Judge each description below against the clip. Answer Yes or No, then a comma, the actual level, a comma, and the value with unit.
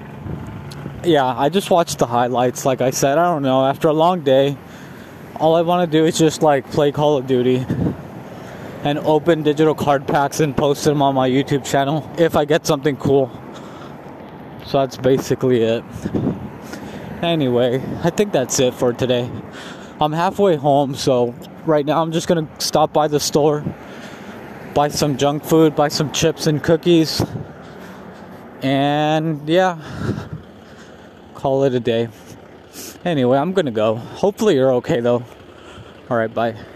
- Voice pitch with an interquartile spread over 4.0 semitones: No, average, 3.7 semitones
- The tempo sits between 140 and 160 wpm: Yes, average, 155 wpm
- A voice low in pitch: No, medium, 145 Hz